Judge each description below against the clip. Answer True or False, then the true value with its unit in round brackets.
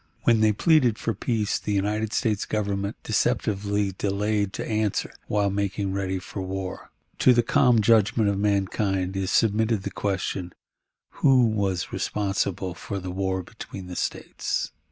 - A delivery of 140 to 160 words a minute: True (150 wpm)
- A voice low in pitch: True (100 Hz)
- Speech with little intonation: True (2.1 semitones)